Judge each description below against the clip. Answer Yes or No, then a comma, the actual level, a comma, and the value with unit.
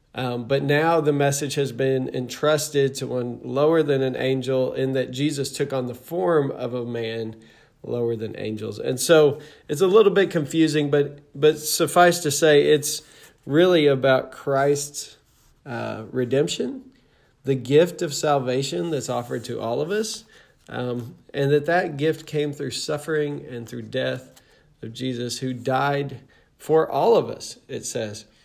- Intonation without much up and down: No, average, 3.3 semitones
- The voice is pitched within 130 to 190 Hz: Yes, medium, 140 Hz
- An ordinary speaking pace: Yes, average, 160 wpm